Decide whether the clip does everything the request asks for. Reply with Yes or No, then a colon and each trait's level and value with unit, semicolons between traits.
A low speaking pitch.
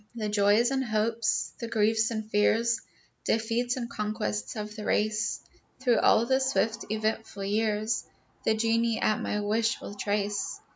No: high, 220 Hz